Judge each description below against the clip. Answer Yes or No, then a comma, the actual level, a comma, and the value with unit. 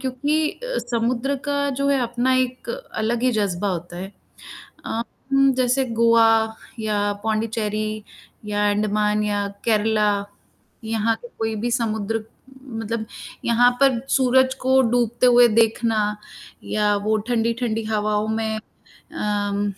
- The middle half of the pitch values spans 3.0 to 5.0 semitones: No, narrow, 2.6 semitones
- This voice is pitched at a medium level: No, high, 225 Hz